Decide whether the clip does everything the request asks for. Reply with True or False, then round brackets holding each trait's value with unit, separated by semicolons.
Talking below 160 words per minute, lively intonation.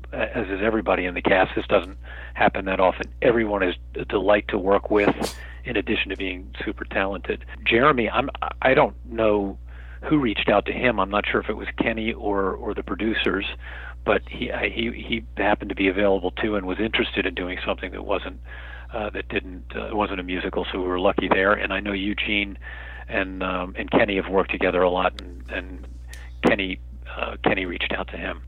False (200 wpm; 8.7 semitones)